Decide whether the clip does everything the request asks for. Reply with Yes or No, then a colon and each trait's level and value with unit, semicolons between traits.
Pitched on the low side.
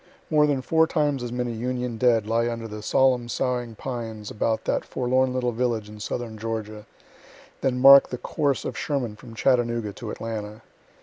Yes: low, 120 Hz